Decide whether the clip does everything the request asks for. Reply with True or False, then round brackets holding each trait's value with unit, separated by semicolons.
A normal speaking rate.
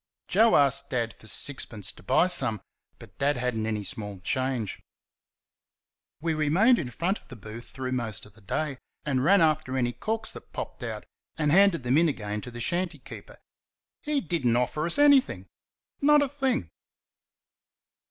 True (175 wpm)